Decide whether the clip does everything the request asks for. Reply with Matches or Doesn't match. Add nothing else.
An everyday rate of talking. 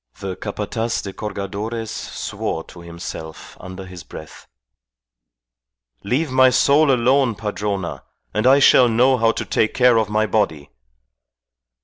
Doesn't match